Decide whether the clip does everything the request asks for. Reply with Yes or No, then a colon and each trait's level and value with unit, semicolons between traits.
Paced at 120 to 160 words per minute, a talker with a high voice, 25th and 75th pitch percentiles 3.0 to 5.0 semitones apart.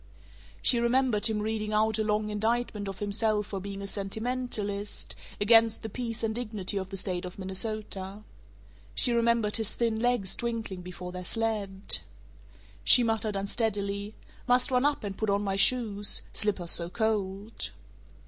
No: average, 155 wpm; high, 210 Hz; narrow, 2.4 semitones